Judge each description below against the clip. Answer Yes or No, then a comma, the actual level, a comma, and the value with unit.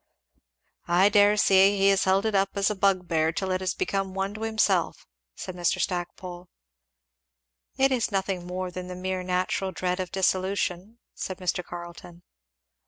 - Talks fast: No, average, 165 wpm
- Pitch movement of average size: No, narrow, 1.6 semitones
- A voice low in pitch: No, medium, 185 Hz